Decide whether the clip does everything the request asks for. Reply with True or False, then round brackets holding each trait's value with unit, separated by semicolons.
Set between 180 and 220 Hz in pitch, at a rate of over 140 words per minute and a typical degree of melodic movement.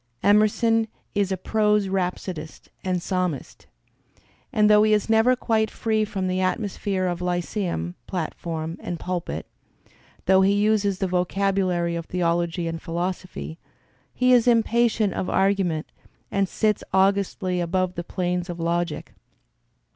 False (185 Hz; 135 wpm; 3.1 semitones)